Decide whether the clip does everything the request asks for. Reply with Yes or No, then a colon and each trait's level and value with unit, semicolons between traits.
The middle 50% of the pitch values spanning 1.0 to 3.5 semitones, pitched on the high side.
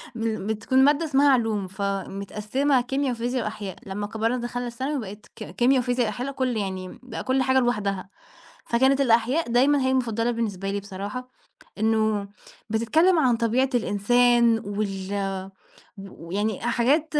No: average, 4.2 semitones; high, 230 Hz